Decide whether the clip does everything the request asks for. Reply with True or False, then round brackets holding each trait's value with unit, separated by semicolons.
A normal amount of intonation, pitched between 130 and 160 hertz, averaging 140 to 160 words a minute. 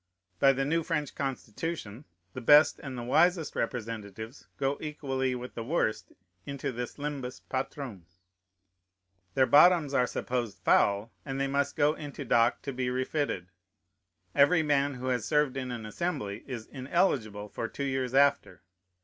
True (3.4 semitones; 135 Hz; 150 wpm)